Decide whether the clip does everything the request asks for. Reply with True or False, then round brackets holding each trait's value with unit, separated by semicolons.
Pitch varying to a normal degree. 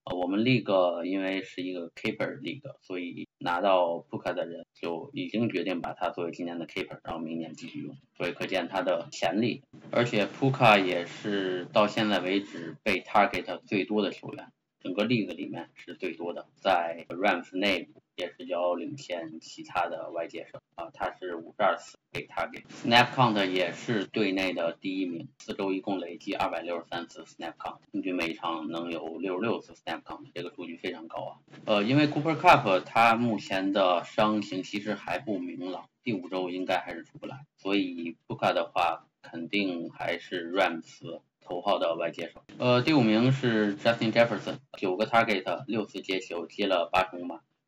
True (5.0 semitones)